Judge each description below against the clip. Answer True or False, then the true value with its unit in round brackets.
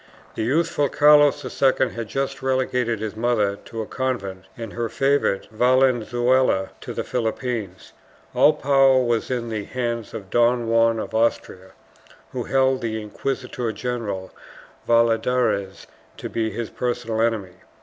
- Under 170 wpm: True (140 wpm)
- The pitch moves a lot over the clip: False (2.9 semitones)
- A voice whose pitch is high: False (120 Hz)